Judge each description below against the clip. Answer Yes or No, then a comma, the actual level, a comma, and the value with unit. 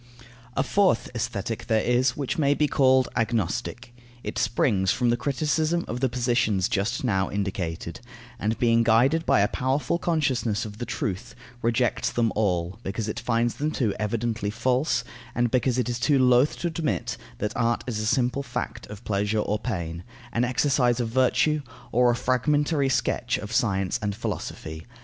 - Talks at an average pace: Yes, average, 170 wpm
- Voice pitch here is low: Yes, low, 120 Hz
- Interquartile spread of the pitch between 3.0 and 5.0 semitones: Yes, average, 3.6 semitones